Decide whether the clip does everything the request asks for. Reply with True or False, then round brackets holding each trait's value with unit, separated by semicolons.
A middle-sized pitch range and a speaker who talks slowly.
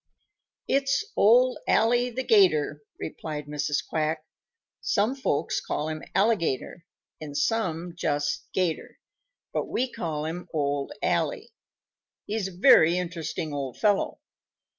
False (6.7 semitones; 120 wpm)